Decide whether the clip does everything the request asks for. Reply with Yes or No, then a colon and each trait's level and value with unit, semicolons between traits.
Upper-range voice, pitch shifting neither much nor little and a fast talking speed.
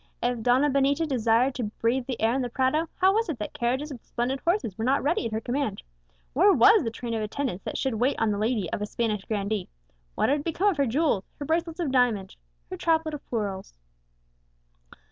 Yes: very high, 255 Hz; average, 5.0 semitones; fast, 220 wpm